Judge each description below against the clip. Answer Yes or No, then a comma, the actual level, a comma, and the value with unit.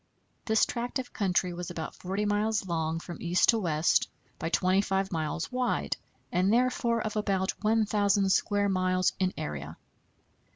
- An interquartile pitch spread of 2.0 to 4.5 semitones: Yes, average, 3.3 semitones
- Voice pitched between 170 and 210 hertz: Yes, high, 190 Hz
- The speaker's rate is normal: Yes, average, 150 wpm